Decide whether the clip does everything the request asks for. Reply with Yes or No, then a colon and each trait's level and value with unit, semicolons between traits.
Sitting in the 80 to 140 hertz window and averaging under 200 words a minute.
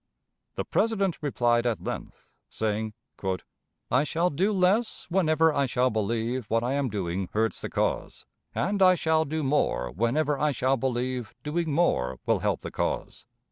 Yes: low, 135 Hz; average, 160 wpm